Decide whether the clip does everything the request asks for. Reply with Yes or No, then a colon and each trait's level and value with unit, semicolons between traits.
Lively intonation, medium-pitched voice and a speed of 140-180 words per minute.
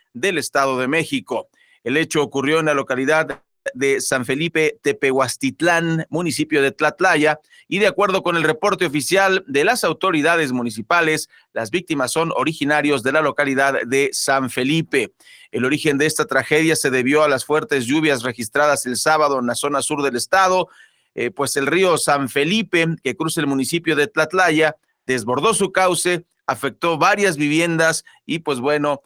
No: average, 3.3 semitones; medium, 150 Hz; average, 165 wpm